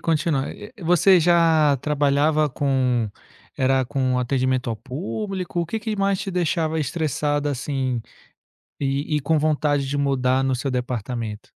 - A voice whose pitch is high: No, medium, 145 Hz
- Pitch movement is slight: No, average, 3.7 semitones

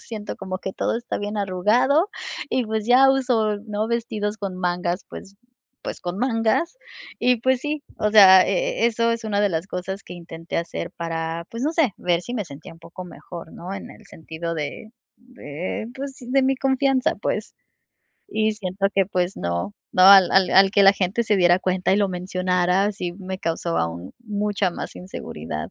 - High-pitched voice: Yes, high, 195 Hz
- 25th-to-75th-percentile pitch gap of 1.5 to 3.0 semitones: No, average, 4.5 semitones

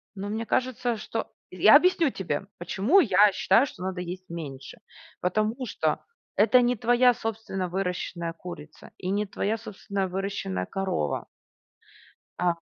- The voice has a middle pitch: No, high, 195 Hz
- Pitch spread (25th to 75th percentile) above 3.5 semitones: Yes, average, 3.9 semitones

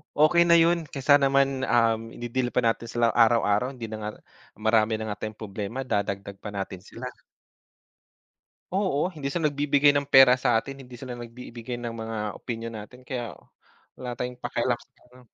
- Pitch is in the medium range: No, low, 120 Hz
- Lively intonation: No, average, 3.4 semitones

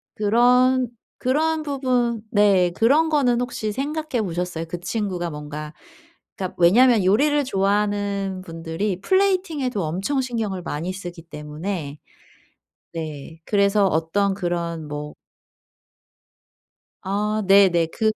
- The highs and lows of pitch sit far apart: Yes, wide, 6.1 semitones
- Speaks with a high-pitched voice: Yes, high, 200 Hz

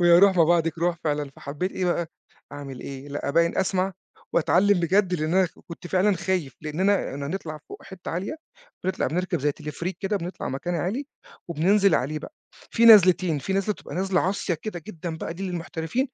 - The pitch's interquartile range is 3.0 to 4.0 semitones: Yes, average, 3.4 semitones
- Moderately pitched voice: Yes, medium, 175 Hz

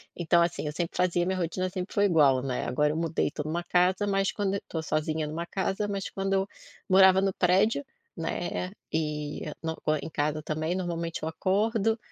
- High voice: No, medium, 175 Hz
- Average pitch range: Yes, average, 3.4 semitones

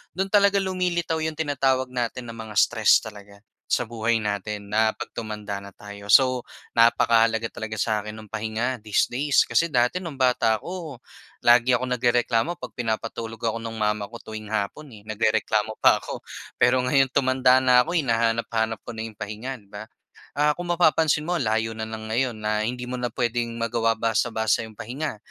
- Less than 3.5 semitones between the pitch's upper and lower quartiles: Yes, average, 3.0 semitones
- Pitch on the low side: Yes, low, 115 Hz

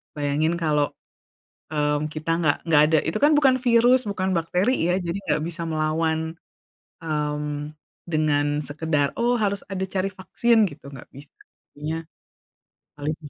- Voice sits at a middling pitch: Yes, medium, 155 Hz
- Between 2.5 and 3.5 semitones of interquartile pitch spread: No, average, 3.9 semitones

